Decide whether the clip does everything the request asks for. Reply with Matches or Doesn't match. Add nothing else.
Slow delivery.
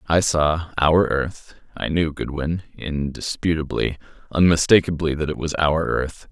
Matches